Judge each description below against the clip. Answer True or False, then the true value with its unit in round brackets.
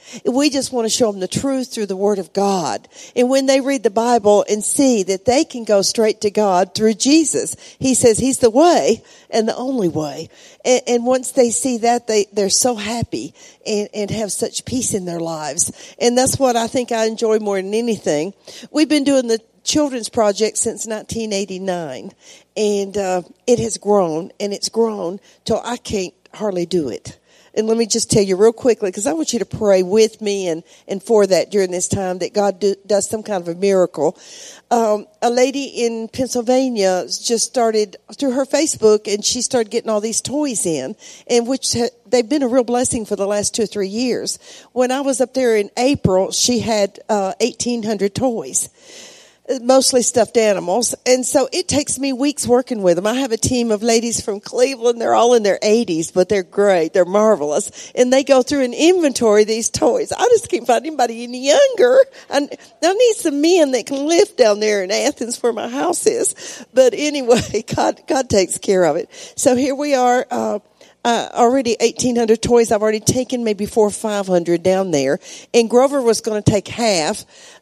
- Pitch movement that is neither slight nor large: True (3.9 semitones)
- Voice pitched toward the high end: True (230 Hz)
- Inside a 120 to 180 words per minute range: False (200 wpm)